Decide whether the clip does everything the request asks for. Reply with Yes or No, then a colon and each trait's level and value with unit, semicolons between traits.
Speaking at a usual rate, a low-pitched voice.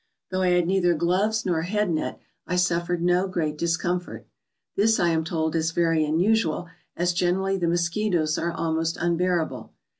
No: average, 170 wpm; medium, 175 Hz